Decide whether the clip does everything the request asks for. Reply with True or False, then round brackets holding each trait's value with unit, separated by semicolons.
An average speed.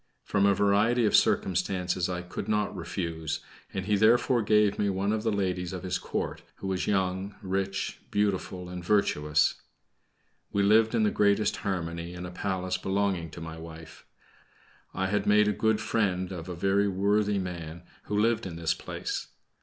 True (175 wpm)